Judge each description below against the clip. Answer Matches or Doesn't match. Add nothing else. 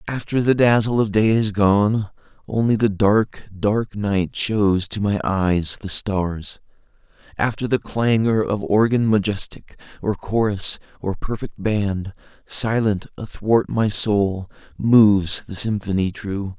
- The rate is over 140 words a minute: Doesn't match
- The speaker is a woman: Doesn't match